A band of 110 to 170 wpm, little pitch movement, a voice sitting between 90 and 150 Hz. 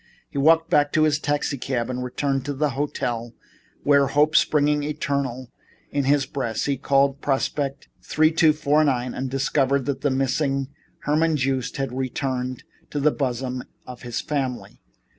Yes: average, 150 wpm; narrow, 2.1 semitones; medium, 140 Hz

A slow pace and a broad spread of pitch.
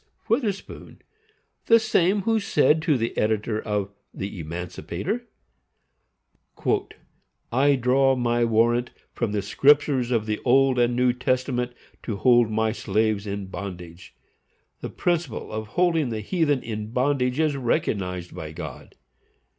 No: slow, 130 wpm; average, 4.9 semitones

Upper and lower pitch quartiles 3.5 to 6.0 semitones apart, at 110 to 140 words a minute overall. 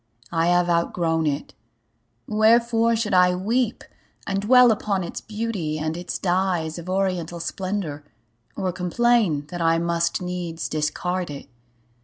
Yes: average, 3.9 semitones; slow, 135 wpm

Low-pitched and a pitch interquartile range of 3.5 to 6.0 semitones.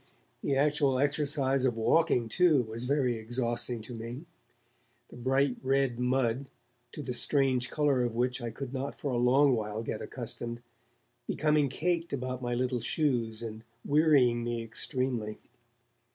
No: low, 130 Hz; average, 2.9 semitones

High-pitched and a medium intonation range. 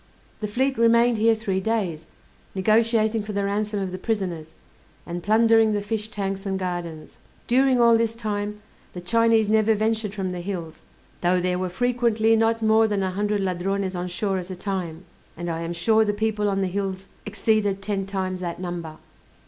Yes: high, 205 Hz; average, 3.2 semitones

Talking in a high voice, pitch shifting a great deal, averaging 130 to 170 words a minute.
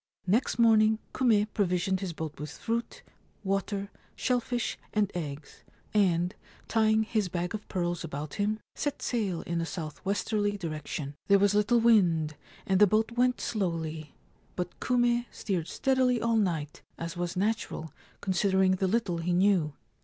No: high, 195 Hz; average, 4.3 semitones; average, 155 wpm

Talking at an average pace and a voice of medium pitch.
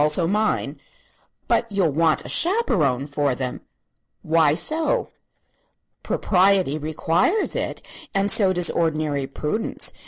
No: slow, 115 wpm; medium, 165 Hz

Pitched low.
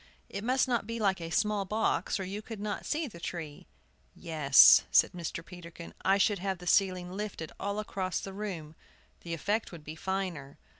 No: high, 190 Hz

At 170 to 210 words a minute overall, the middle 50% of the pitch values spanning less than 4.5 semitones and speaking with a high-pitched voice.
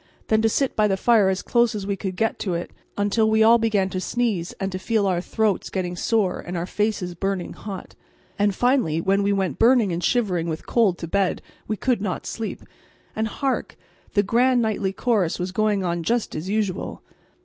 Yes: fast, 205 wpm; average, 3.2 semitones; high, 200 Hz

